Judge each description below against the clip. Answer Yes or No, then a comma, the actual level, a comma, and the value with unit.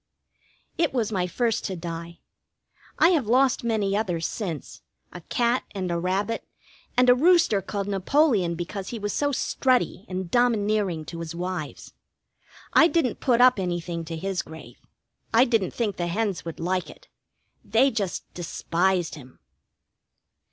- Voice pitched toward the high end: Yes, high, 195 Hz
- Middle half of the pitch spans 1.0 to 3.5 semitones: No, wide, 5.5 semitones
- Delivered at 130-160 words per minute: Yes, average, 150 wpm